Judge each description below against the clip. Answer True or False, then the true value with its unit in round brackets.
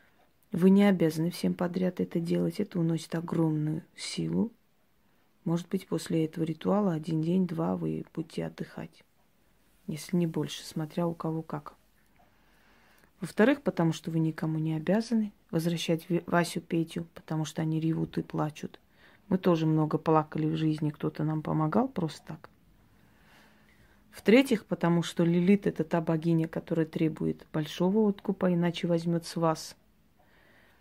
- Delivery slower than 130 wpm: False (135 wpm)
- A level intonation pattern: True (2.3 semitones)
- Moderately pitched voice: True (170 Hz)